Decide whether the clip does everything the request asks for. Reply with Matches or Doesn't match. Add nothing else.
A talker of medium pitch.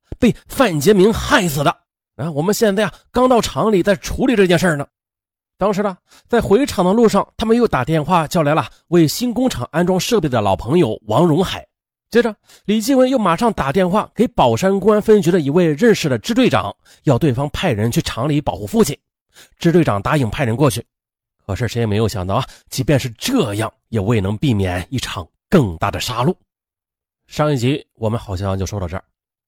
Matches